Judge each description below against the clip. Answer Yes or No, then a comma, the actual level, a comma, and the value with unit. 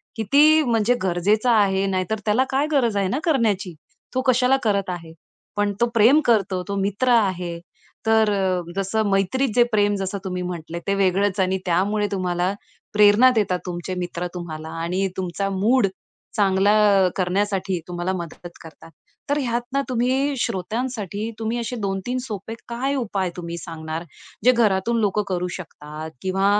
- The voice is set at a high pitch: Yes, high, 200 Hz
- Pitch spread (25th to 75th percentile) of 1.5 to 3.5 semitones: No, average, 3.9 semitones